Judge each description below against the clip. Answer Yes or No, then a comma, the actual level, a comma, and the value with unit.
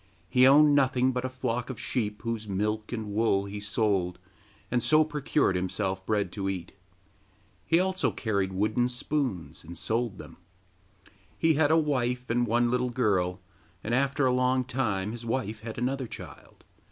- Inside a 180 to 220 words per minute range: No, average, 165 wpm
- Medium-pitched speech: No, low, 120 Hz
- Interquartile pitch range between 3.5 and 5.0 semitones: Yes, average, 3.9 semitones